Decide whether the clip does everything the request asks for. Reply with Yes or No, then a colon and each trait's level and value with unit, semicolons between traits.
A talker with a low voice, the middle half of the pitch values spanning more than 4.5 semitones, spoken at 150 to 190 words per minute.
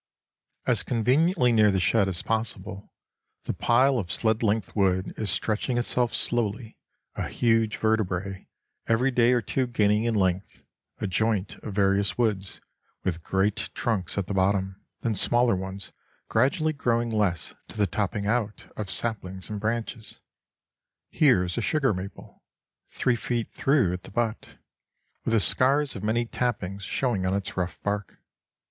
No: low, 110 Hz; average, 3.5 semitones; average, 155 wpm